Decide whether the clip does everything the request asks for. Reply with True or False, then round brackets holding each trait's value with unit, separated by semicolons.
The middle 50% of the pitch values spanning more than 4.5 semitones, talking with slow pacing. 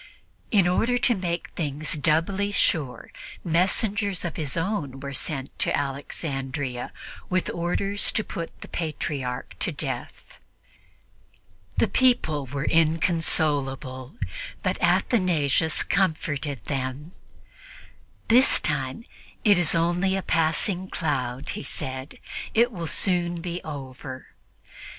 True (4.9 semitones; 110 wpm)